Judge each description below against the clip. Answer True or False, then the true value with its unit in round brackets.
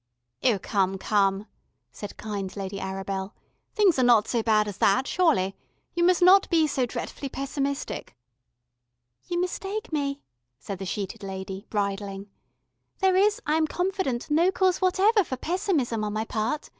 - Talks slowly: False (155 wpm)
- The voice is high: True (245 Hz)